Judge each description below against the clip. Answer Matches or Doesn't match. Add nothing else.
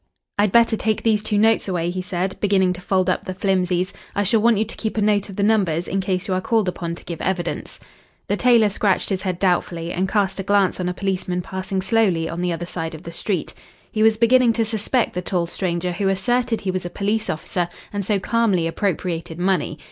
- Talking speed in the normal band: Doesn't match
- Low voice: Doesn't match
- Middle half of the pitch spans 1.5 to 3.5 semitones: Matches